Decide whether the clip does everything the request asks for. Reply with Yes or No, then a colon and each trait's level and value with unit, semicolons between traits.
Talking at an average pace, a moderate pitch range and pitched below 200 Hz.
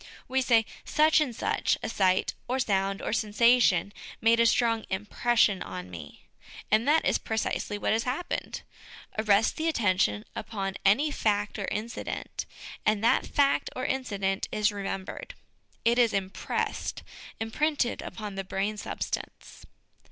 No: average, 145 wpm; average, 3.5 semitones; high, 215 Hz